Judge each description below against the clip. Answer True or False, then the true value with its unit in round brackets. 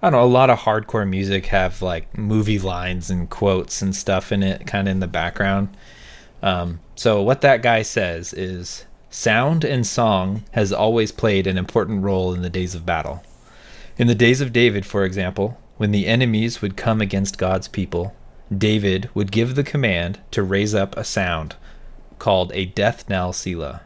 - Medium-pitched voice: False (100 Hz)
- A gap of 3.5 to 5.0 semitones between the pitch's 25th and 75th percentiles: False (3.1 semitones)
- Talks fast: False (185 wpm)